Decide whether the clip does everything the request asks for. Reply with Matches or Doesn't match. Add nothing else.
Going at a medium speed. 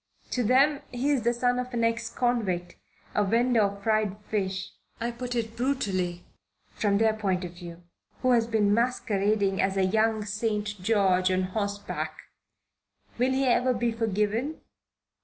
Matches